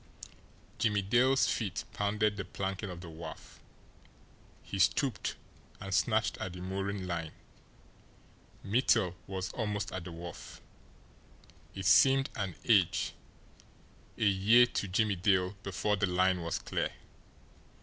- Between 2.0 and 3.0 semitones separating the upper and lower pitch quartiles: Yes, average, 2.7 semitones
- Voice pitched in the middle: No, very low, 95 Hz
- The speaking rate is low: Yes, slow, 125 wpm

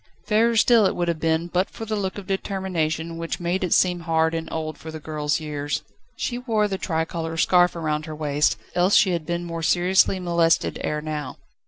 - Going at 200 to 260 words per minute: Yes, fast, 205 wpm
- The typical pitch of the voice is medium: Yes, medium, 170 Hz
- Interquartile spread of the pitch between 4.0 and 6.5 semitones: No, average, 3.0 semitones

